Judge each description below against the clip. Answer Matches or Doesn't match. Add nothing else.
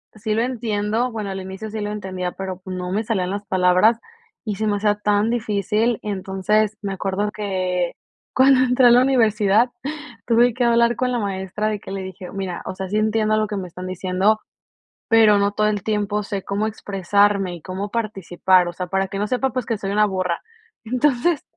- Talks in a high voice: Matches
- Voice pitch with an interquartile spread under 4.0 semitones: Matches